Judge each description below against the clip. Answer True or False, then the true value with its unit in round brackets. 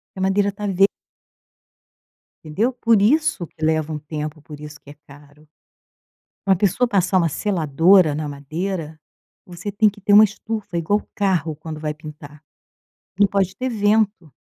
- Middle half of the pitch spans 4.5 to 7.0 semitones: True (5.0 semitones)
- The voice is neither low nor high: True (180 Hz)